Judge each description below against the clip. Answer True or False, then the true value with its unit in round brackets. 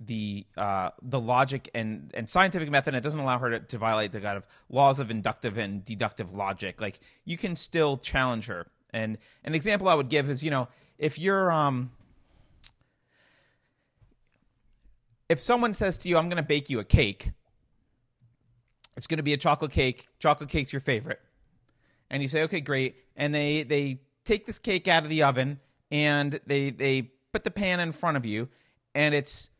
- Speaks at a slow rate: False (180 wpm)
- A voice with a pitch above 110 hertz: True (135 Hz)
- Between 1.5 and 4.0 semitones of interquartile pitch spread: False (4.8 semitones)